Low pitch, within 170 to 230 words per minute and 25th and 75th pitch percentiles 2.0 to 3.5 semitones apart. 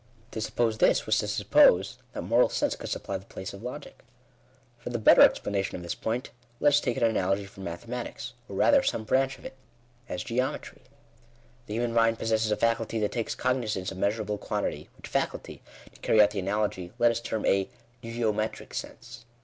Yes: low, 110 Hz; average, 190 wpm; average, 3.1 semitones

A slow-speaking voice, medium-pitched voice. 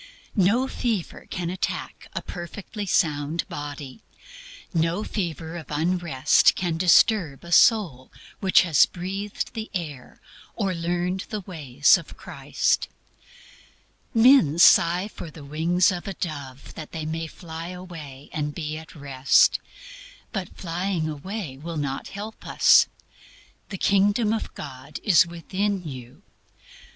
Yes: slow, 130 wpm; medium, 170 Hz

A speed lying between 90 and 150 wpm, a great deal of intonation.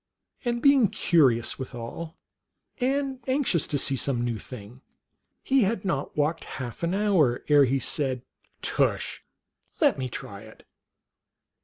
Yes: average, 140 wpm; wide, 8.9 semitones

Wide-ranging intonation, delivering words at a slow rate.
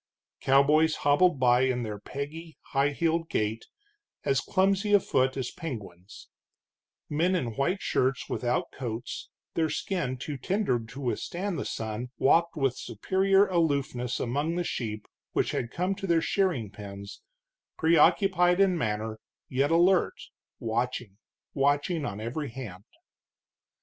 Yes: wide, 6.2 semitones; slow, 130 wpm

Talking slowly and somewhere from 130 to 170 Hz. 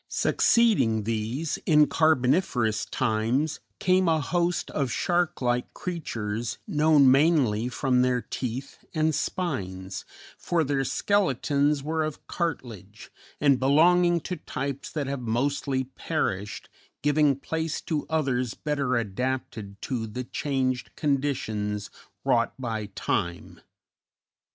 Yes: slow, 110 wpm; low, 135 Hz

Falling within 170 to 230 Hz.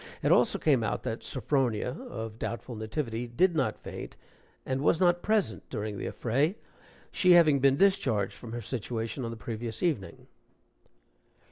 No: low, 120 Hz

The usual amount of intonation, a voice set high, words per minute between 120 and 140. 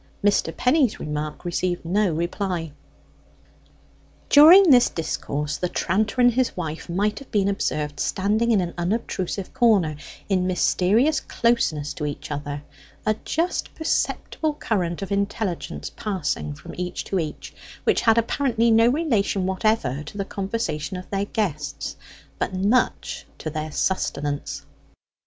No: wide, 5.7 semitones; high, 195 Hz; slow, 135 wpm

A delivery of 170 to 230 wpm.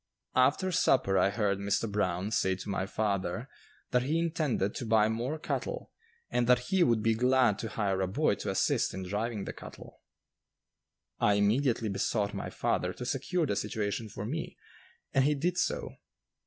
Yes: average, 175 wpm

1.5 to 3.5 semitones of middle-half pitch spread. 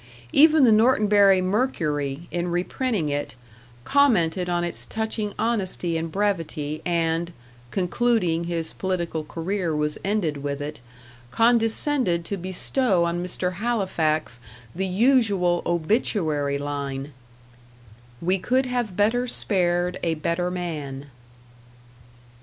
No: average, 4.7 semitones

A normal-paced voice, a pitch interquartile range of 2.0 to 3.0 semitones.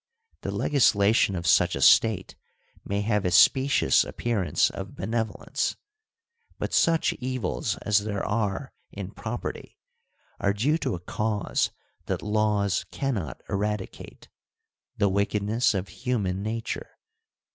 No: slow, 120 wpm; average, 2.7 semitones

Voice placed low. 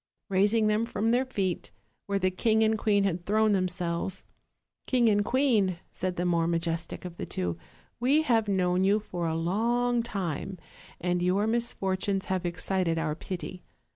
No: high, 190 Hz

